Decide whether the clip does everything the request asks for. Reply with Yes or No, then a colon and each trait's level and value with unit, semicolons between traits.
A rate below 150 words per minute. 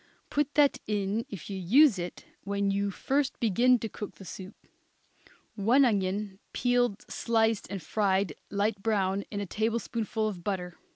No: average, 155 wpm